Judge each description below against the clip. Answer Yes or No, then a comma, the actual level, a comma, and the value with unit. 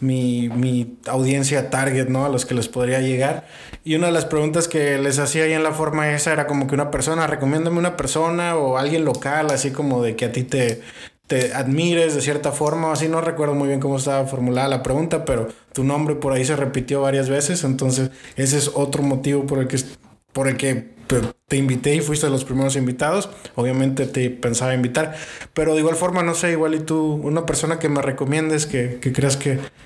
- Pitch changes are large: No, average, 2.9 semitones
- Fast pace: Yes, fast, 215 wpm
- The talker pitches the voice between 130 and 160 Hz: Yes, medium, 140 Hz